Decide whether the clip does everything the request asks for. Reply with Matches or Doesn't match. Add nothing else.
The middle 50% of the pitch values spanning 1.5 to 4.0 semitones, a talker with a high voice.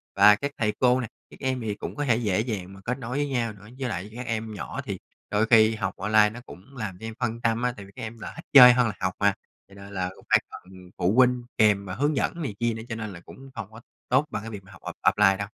Doesn't match